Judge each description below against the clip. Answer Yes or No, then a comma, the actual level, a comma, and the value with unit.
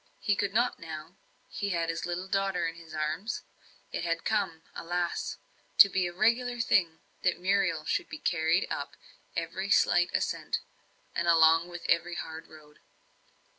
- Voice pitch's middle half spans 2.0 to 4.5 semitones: Yes, average, 3.2 semitones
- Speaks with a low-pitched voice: No, medium, 175 Hz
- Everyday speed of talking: Yes, average, 155 wpm